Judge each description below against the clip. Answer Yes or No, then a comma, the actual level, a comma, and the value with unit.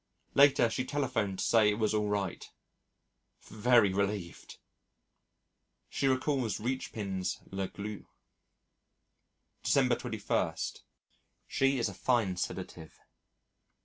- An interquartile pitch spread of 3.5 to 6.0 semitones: Yes, average, 4.3 semitones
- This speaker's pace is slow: Yes, slow, 100 wpm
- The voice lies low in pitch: Yes, low, 105 Hz